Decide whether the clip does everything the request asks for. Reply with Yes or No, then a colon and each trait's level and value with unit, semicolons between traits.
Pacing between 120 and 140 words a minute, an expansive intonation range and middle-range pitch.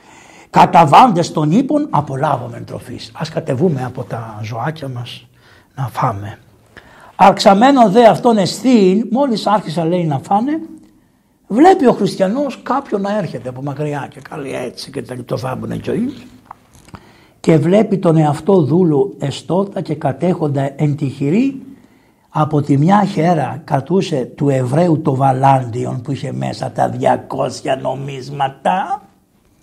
Yes: average, 125 wpm; wide, 6.9 semitones; medium, 160 Hz